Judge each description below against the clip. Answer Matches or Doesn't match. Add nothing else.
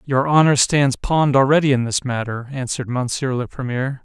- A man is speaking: Matches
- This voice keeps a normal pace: Matches